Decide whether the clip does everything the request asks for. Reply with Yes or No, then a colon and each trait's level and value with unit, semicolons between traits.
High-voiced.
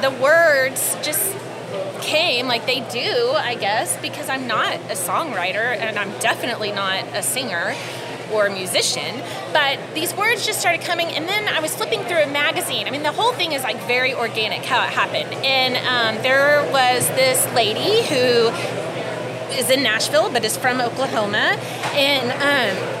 Yes: very high, 275 Hz